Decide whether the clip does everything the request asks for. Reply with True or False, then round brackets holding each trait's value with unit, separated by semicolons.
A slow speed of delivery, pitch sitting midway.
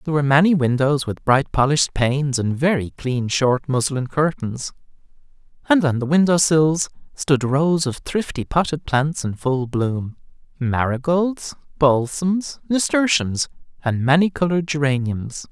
True (130 wpm; 145 Hz)